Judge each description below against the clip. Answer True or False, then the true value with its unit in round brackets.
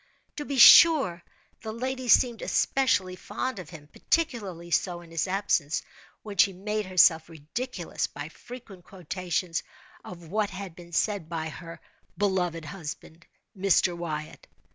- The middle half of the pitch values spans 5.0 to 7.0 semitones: False (4.3 semitones)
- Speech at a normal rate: False (130 wpm)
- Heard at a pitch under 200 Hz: True (185 Hz)